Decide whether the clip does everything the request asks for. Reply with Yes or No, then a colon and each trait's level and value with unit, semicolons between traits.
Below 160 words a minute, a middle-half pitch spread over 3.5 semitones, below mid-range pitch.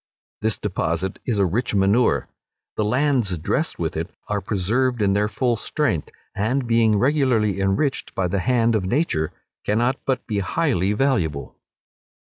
Yes: average, 150 wpm; average, 4.4 semitones; low, 105 Hz